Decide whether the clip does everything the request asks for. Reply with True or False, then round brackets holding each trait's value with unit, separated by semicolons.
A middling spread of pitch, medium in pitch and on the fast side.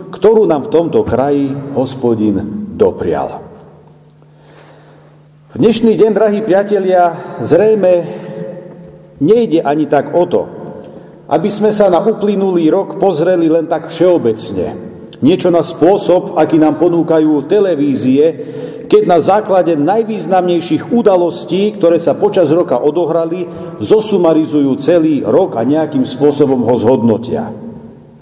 False (4.7 semitones; 170 Hz; 115 wpm)